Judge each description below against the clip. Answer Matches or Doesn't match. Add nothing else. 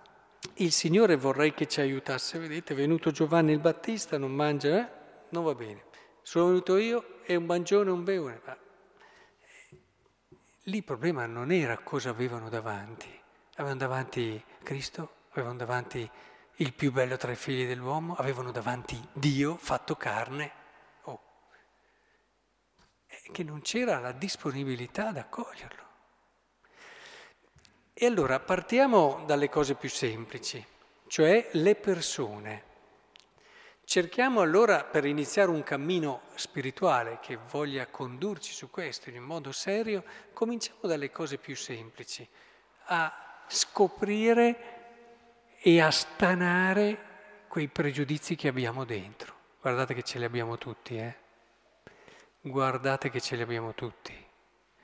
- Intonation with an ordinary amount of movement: Doesn't match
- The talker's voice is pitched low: Doesn't match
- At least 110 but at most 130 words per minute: Matches